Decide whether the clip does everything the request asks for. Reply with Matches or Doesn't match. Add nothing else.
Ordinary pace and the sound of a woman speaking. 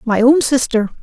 Matches